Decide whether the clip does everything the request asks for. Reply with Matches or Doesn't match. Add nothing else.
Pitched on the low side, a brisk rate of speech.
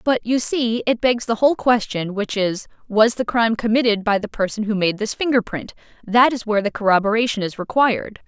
Doesn't match